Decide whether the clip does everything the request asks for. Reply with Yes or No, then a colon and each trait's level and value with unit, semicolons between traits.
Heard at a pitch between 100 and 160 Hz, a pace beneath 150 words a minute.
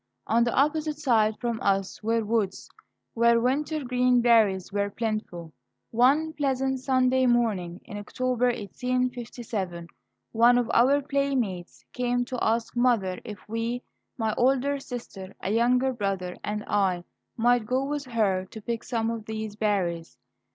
No: high, 235 Hz; average, 140 wpm